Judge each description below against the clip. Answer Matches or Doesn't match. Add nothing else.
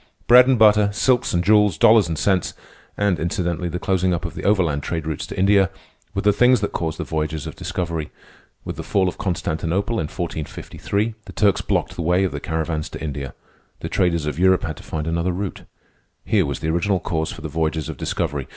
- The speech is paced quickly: Matches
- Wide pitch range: Doesn't match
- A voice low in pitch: Matches